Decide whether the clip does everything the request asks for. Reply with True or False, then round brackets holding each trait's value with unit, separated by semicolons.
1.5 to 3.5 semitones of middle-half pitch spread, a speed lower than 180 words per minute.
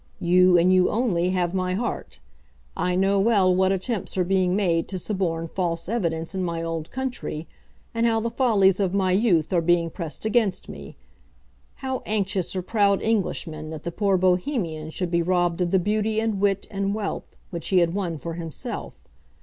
False (3.0 semitones; 185 wpm)